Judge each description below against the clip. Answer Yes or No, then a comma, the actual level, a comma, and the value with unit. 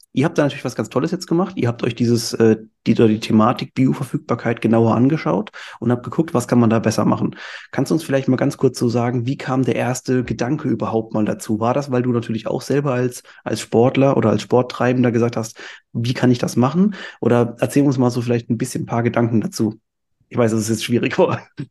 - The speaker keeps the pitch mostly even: Yes, narrow, 2.3 semitones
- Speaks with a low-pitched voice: Yes, low, 120 Hz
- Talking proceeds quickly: Yes, fast, 230 wpm